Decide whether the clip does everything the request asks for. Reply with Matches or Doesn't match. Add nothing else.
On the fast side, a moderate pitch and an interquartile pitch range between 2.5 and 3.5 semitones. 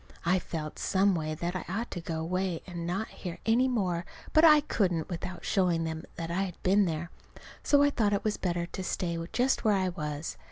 Matches